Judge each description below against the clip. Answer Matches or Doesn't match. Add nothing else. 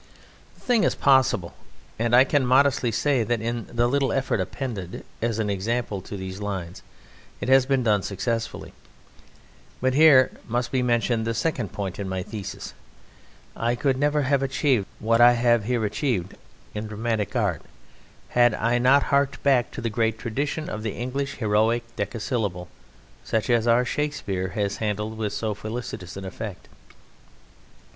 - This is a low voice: Matches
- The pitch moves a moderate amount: Matches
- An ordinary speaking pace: Matches